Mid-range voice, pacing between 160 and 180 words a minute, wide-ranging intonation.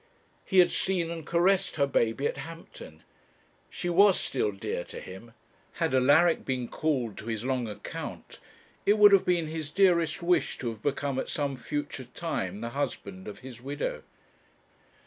Yes: medium, 145 Hz; average, 165 wpm; wide, 6.1 semitones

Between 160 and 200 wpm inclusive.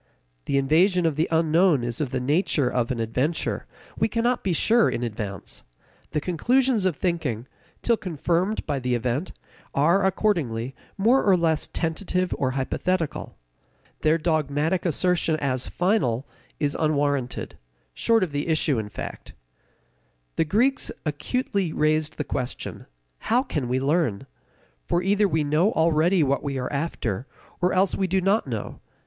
No: average, 150 wpm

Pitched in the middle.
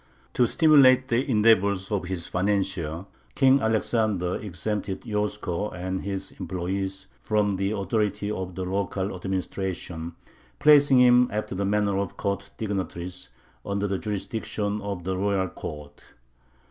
No: low, 100 Hz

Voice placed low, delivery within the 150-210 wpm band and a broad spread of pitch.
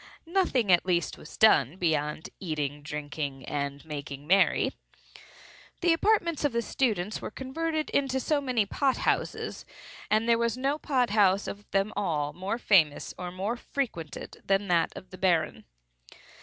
No: high, 195 Hz; average, 155 wpm; wide, 8.4 semitones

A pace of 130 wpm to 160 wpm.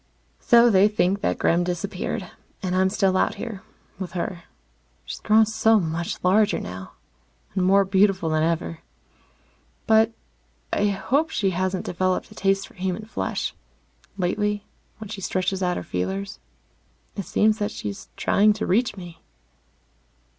Yes: average, 145 wpm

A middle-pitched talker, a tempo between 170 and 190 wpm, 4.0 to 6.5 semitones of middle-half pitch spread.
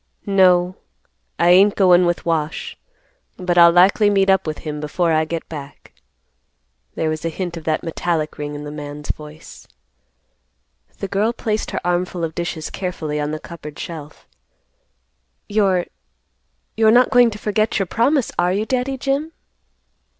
No: medium, 175 Hz; average, 155 wpm; average, 4.4 semitones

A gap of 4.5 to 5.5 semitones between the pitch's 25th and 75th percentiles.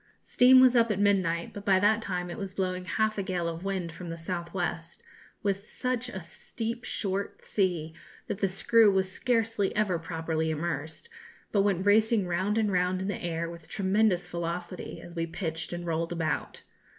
No: average, 3.3 semitones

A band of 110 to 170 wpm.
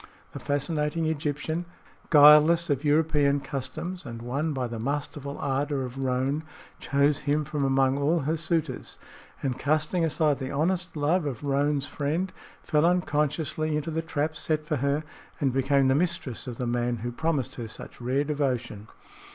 Yes: average, 160 wpm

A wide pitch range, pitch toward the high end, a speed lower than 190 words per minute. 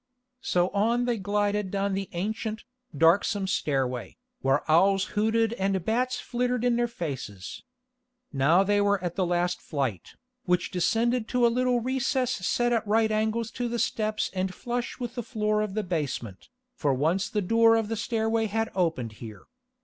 No: average, 4.5 semitones; high, 210 Hz; average, 170 wpm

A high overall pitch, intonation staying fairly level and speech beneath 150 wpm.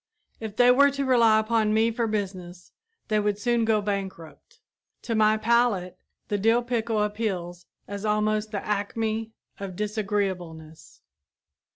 Yes: high, 215 Hz; narrow, 2.3 semitones; average, 140 wpm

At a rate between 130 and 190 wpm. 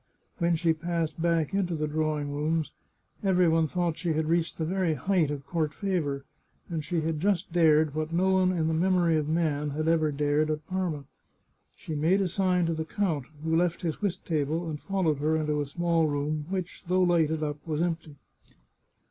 No: average, 200 wpm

